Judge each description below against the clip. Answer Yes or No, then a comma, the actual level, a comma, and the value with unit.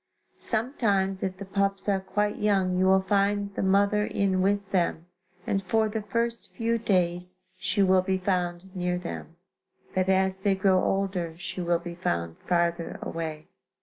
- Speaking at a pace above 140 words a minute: Yes, average, 165 wpm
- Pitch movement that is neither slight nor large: No, narrow, 2.0 semitones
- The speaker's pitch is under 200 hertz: Yes, high, 190 Hz